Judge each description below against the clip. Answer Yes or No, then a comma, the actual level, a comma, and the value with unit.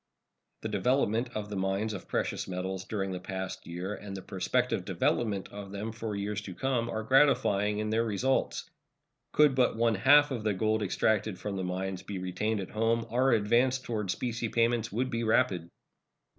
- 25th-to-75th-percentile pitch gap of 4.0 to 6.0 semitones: No, average, 3.3 semitones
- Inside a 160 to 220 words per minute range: Yes, average, 185 wpm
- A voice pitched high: No, low, 110 Hz